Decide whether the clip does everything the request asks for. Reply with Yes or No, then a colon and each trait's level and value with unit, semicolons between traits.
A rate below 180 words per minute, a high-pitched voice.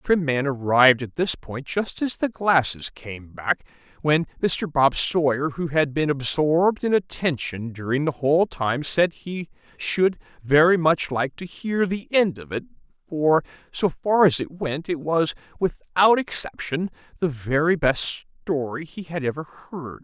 No: average, 170 wpm; medium, 155 Hz